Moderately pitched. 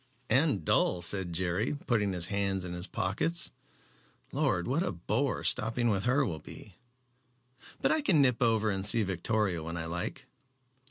No: low, 100 Hz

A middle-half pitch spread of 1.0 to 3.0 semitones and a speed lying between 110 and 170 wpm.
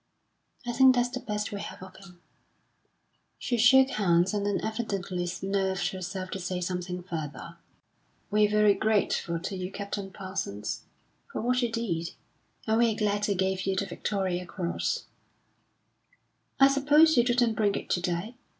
No: average, 3.7 semitones; average, 160 wpm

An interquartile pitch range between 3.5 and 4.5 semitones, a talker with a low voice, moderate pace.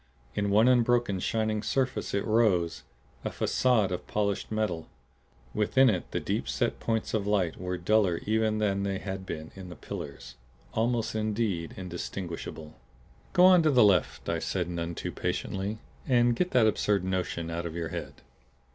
Yes: average, 3.9 semitones; low, 100 Hz; average, 165 wpm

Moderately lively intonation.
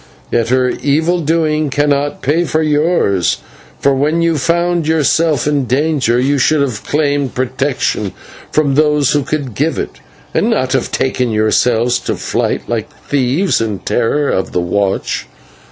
Yes: average, 3.7 semitones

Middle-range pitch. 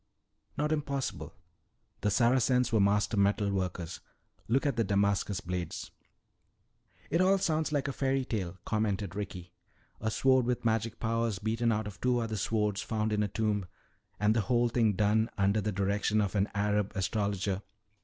No: low, 105 Hz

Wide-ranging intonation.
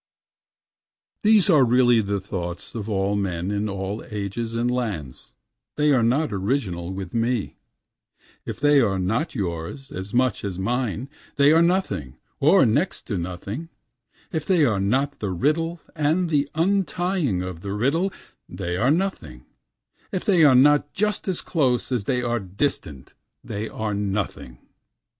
Yes: wide, 7.0 semitones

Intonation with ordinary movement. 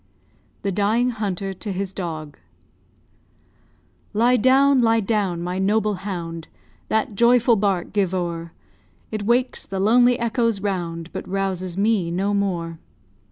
Yes: average, 3.9 semitones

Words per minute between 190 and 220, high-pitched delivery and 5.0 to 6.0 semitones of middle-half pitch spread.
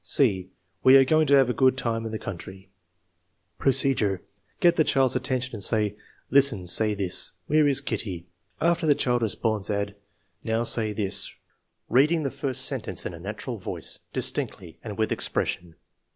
No: average, 195 wpm; low, 115 Hz; wide, 5.6 semitones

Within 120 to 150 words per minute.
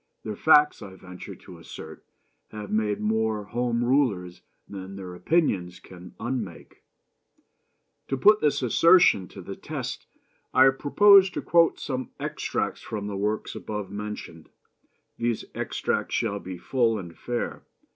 Yes: slow, 135 wpm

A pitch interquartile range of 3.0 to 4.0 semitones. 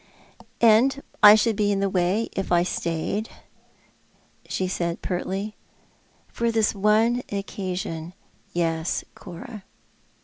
Yes: average, 3.5 semitones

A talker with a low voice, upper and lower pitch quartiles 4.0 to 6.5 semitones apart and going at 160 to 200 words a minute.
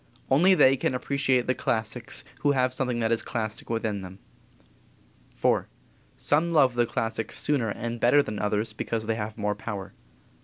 No: low, 115 Hz; average, 3.2 semitones; average, 165 wpm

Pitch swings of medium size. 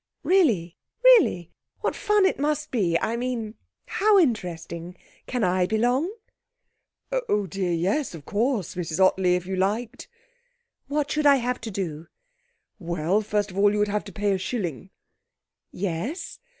No: wide, 6.3 semitones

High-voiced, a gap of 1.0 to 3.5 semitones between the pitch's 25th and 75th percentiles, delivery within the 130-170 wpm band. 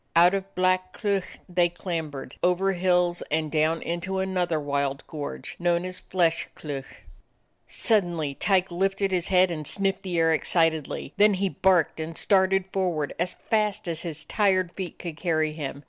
No: medium, 175 Hz; average, 2.9 semitones; average, 160 wpm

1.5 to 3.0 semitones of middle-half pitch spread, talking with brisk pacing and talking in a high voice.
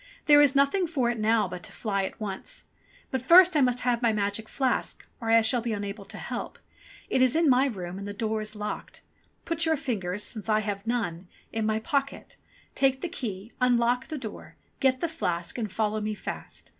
No: average, 4.2 semitones; fast, 210 wpm; high, 230 Hz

